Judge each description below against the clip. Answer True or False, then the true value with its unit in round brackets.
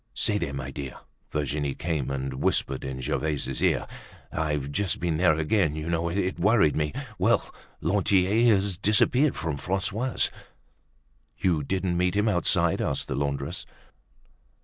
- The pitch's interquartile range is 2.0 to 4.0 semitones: False (5.2 semitones)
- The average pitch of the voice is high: False (85 Hz)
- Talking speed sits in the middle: True (145 wpm)